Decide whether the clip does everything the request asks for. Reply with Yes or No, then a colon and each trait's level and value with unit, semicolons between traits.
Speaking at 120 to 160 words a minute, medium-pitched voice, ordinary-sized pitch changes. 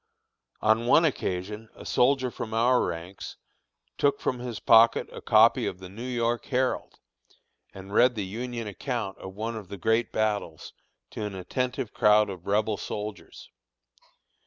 No: average, 155 wpm; low, 110 Hz; average, 3.5 semitones